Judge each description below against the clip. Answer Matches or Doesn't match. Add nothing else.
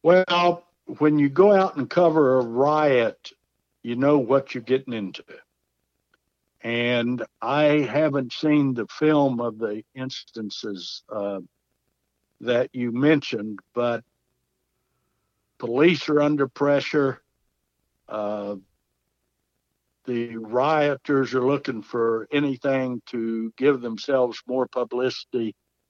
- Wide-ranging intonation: Doesn't match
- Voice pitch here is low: Matches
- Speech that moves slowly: Matches